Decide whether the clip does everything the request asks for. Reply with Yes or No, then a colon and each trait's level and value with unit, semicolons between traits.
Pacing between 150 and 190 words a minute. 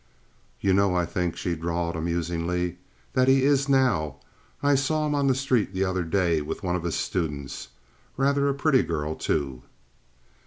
Yes: average, 165 wpm